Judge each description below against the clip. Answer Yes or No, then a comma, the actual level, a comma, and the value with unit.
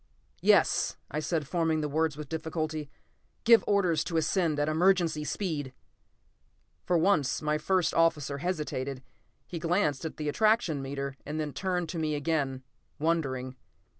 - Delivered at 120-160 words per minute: Yes, average, 145 wpm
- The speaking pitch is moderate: Yes, medium, 155 Hz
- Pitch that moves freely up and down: No, narrow, 2.6 semitones